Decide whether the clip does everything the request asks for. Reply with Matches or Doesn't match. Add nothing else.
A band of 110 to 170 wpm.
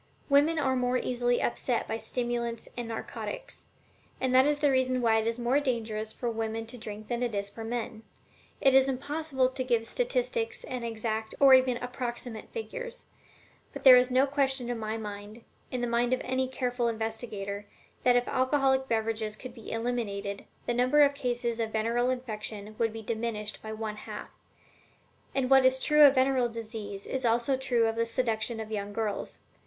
Doesn't match